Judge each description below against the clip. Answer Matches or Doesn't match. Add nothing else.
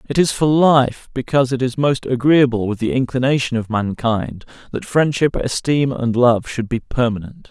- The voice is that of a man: Matches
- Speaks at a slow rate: Doesn't match